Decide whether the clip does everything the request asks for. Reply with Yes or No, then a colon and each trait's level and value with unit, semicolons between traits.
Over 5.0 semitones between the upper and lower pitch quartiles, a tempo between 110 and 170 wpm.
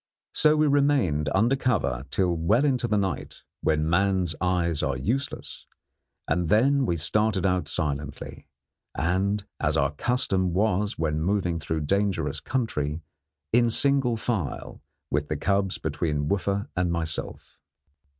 Yes: wide, 5.6 semitones; slow, 135 wpm